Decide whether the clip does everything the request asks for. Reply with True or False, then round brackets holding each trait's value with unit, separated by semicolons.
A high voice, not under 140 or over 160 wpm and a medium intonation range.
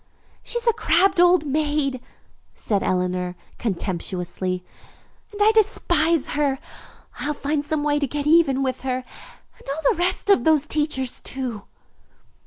True (290 Hz; 145 wpm; 4.6 semitones)